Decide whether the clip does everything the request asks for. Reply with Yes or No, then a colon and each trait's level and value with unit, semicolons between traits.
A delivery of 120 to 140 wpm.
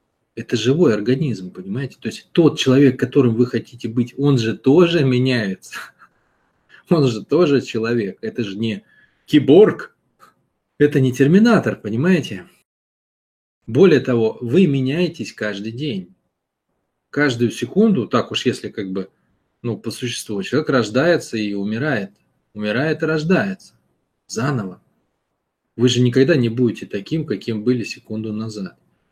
Yes: average, 130 wpm